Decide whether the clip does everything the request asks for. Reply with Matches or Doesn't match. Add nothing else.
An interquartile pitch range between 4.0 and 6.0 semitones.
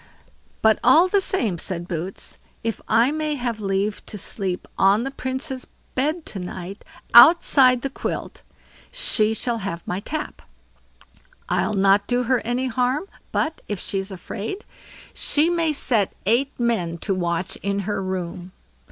Matches